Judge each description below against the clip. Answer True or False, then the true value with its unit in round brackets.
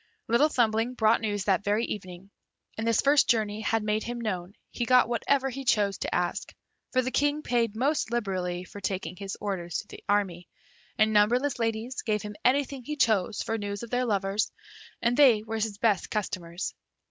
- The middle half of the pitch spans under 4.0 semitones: True (3.1 semitones)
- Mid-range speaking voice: False (220 Hz)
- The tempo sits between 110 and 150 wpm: False (190 wpm)